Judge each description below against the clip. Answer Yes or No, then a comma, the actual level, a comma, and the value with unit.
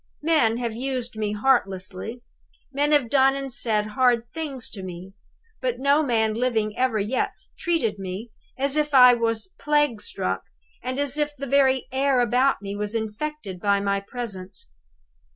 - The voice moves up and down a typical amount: Yes, average, 4.5 semitones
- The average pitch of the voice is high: Yes, high, 245 Hz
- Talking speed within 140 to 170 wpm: Yes, average, 160 wpm